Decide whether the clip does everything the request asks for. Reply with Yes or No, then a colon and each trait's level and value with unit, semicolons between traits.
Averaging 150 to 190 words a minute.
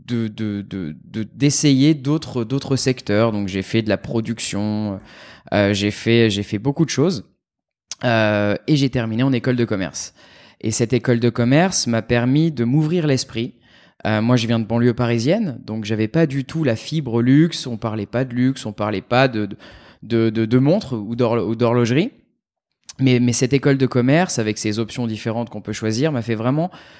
No: average, 200 wpm